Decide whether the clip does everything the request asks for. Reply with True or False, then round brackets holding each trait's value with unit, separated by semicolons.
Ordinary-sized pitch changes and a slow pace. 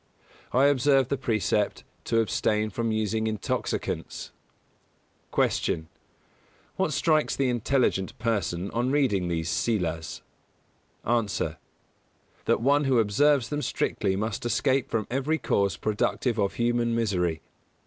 True (4.5 semitones; 120 wpm)